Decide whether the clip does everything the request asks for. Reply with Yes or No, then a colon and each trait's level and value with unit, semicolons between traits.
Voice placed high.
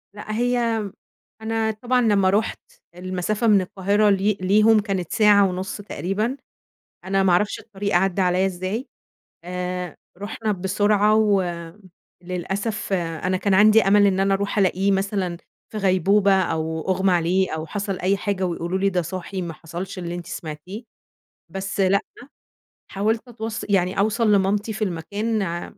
Yes: high, 195 Hz